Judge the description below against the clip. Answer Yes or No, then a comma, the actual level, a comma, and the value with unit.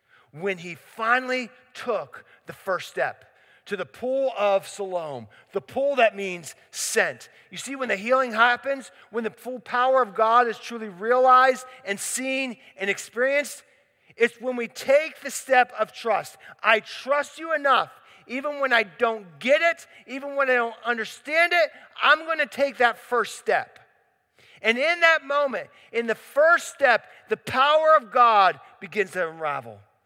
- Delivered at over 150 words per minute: Yes, average, 165 wpm